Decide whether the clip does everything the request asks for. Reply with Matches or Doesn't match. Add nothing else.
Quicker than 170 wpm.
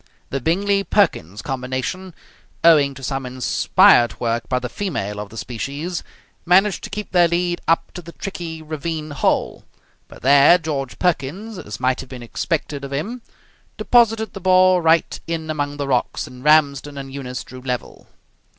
Doesn't match